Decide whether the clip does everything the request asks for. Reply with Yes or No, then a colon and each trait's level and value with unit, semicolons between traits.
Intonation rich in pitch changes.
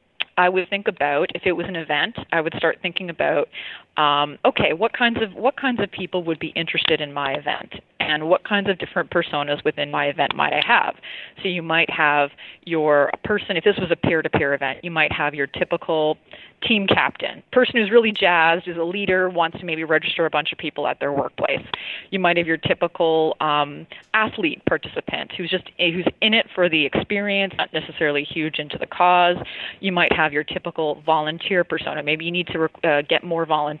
No: average, 3.3 semitones